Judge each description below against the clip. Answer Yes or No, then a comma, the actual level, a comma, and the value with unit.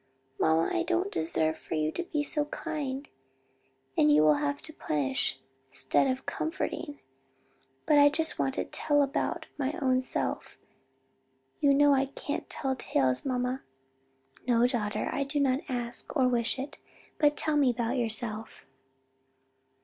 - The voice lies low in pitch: No, very high, 265 Hz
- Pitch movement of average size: Yes, average, 4.6 semitones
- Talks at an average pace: Yes, average, 150 wpm